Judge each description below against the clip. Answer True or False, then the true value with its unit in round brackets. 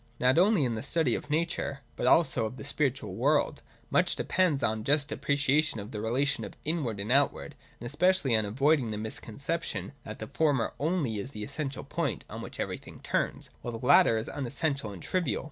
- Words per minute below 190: False (195 wpm)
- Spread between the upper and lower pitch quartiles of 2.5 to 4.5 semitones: False (5.3 semitones)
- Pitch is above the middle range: False (135 Hz)